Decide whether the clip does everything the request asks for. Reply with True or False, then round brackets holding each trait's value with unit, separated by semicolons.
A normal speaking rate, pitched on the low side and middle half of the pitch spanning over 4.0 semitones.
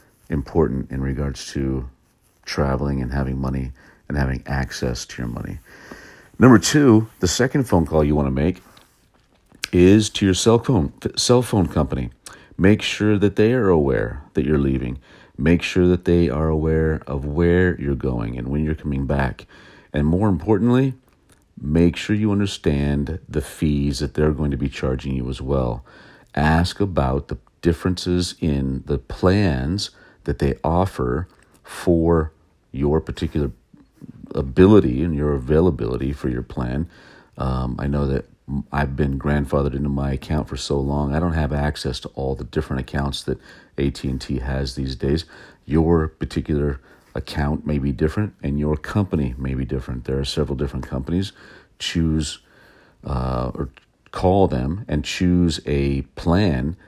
True (155 wpm; 75 Hz; 4.6 semitones)